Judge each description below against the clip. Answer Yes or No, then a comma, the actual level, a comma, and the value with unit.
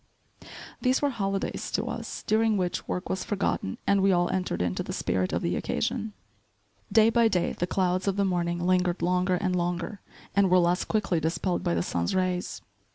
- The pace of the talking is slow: No, average, 190 wpm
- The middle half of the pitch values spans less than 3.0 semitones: Yes, narrow, 2.4 semitones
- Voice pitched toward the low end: No, medium, 185 Hz